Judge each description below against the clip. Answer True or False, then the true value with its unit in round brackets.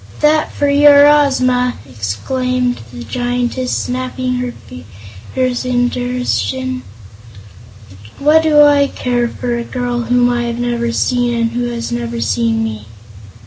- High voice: True (245 Hz)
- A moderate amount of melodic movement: False (1.7 semitones)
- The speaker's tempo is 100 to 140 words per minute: True (135 wpm)